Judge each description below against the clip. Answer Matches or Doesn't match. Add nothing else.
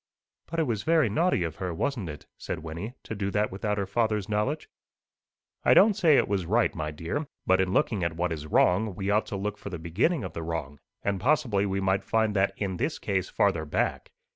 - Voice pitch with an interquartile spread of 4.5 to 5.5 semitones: Doesn't match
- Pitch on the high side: Doesn't match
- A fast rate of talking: Matches